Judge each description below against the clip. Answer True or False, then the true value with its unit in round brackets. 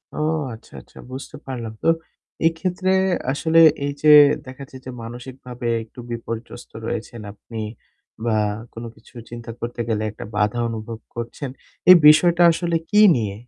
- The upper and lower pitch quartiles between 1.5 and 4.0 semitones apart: False (4.7 semitones)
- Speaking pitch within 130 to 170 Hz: False (120 Hz)